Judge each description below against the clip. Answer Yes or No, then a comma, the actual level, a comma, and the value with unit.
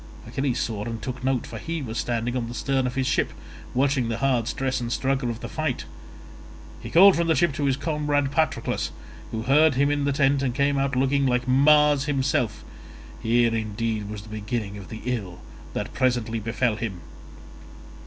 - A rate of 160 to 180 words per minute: No, average, 190 wpm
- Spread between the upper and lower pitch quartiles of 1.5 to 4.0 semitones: Yes, average, 3.4 semitones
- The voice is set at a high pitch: No, low, 130 Hz